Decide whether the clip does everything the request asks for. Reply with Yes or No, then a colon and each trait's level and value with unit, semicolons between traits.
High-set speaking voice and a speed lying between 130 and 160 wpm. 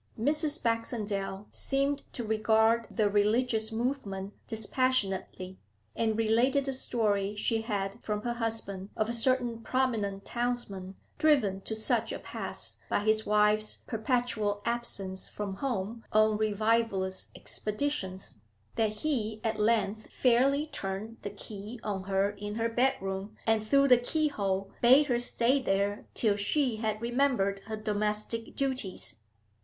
Yes: high, 220 Hz; slow, 135 wpm